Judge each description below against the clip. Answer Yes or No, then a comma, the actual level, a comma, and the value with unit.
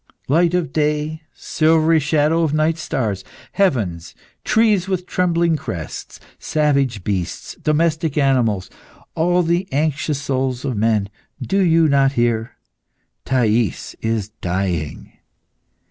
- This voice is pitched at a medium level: Yes, medium, 145 Hz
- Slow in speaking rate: Yes, slow, 115 wpm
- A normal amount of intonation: No, wide, 6.2 semitones